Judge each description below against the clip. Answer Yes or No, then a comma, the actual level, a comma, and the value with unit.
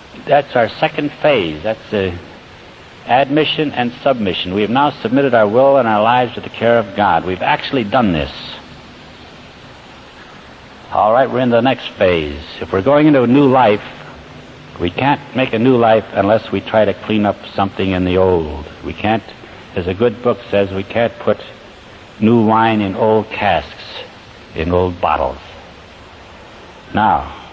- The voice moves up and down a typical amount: Yes, average, 4.2 semitones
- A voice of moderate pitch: No, low, 110 Hz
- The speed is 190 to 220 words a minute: No, average, 165 wpm